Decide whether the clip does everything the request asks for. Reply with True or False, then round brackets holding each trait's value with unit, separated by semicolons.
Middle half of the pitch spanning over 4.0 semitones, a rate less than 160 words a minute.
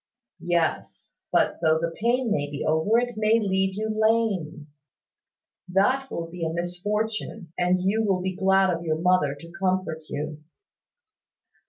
True (4.4 semitones; 150 wpm)